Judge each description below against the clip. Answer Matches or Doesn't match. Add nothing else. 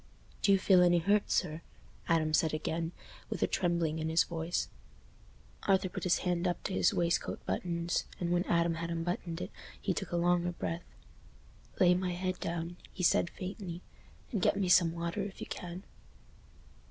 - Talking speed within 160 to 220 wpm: Matches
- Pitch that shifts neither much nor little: Doesn't match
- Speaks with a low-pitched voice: Doesn't match